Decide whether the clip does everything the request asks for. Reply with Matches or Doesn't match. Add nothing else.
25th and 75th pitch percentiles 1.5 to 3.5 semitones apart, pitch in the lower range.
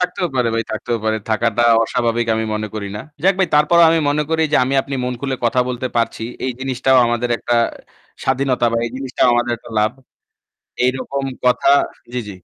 Matches